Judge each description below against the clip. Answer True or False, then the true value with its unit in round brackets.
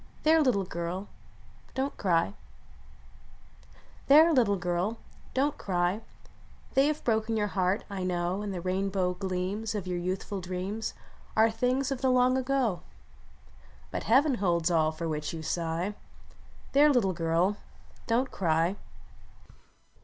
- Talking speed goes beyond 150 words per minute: False (140 wpm)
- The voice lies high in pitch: True (195 Hz)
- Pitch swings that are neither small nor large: False (5.7 semitones)